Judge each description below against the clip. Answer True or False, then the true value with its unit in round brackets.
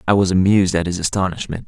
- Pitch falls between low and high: False (95 Hz)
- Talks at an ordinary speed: False (215 wpm)